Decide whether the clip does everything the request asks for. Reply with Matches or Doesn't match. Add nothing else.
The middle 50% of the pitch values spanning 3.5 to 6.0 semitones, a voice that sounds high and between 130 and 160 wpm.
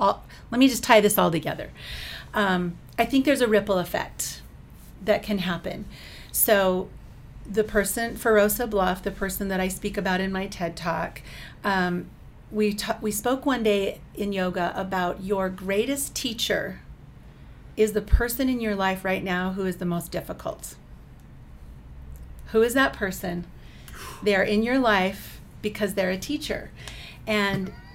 Doesn't match